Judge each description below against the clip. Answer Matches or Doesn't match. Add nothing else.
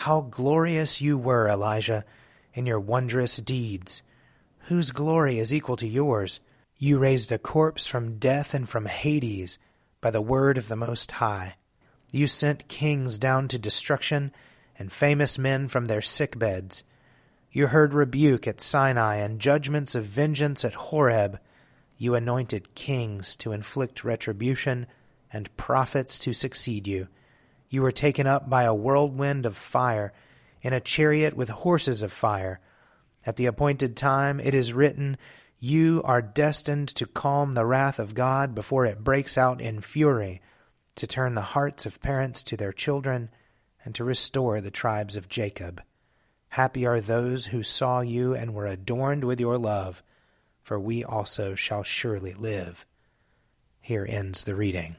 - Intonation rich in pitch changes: Doesn't match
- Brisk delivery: Doesn't match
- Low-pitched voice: Matches